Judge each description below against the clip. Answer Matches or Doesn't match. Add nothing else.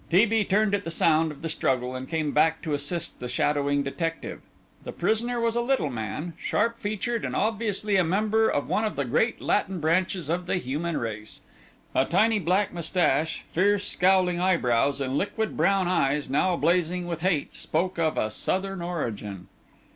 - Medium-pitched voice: Matches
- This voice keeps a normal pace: Matches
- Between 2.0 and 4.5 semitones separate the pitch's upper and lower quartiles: Doesn't match